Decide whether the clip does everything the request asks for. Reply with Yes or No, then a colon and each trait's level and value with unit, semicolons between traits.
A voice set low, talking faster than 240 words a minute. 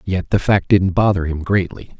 No: very low, 90 Hz; fast, 210 wpm